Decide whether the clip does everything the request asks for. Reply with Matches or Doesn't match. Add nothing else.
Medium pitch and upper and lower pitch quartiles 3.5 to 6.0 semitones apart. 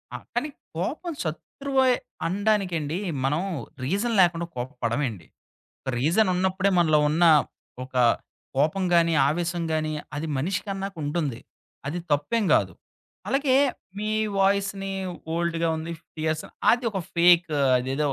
Matches